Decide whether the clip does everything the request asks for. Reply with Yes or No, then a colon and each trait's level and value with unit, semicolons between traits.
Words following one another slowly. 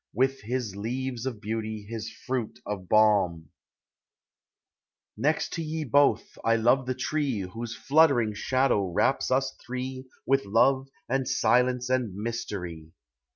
Yes: slow, 130 wpm